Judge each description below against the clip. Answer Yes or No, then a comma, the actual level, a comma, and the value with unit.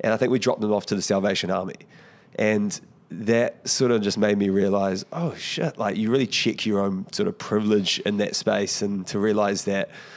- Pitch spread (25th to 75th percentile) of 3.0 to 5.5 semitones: No, narrow, 2.5 semitones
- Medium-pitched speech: No, low, 105 Hz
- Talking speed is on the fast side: Yes, fast, 220 wpm